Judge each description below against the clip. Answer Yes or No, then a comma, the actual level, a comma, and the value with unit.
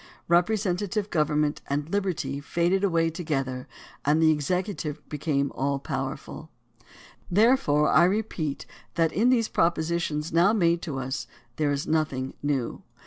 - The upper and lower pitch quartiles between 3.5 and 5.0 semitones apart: Yes, average, 3.8 semitones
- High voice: No, medium, 160 Hz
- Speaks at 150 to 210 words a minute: No, average, 140 wpm